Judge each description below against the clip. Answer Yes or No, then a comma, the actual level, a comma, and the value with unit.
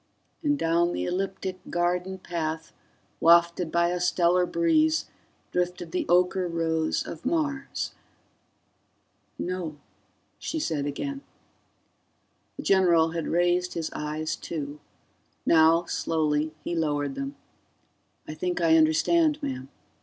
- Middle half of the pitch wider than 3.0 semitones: No, narrow, 2.4 semitones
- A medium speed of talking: No, slow, 115 wpm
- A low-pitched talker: No, medium, 170 Hz